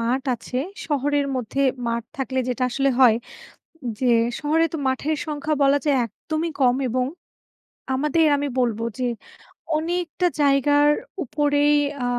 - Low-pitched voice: No, very high, 280 Hz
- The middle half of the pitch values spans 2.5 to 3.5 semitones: Yes, average, 2.8 semitones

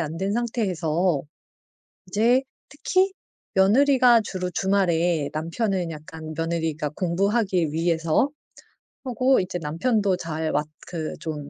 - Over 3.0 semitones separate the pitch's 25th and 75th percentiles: Yes, average, 5.1 semitones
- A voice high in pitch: No, medium, 180 Hz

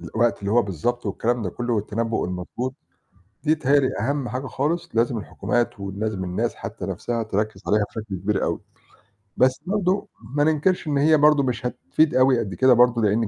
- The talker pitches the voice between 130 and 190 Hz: No, low, 120 Hz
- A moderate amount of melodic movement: Yes, average, 4.4 semitones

